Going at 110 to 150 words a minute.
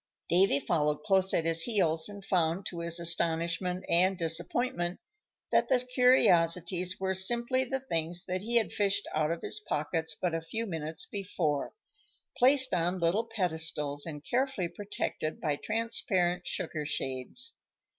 Yes: average, 145 wpm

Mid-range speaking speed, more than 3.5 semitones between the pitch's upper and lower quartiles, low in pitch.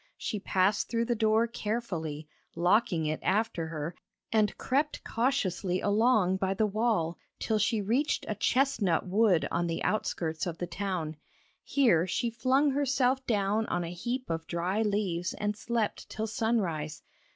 No: average, 150 wpm; average, 5.0 semitones; high, 210 Hz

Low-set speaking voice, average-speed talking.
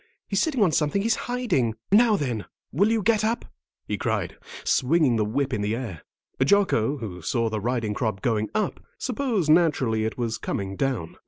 Yes: low, 130 Hz; average, 180 wpm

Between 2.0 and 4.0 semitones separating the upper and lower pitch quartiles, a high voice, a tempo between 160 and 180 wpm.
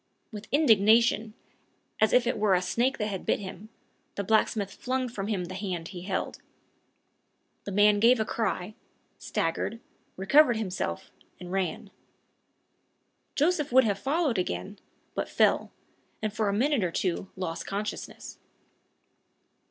No: average, 3.7 semitones; high, 210 Hz; average, 140 wpm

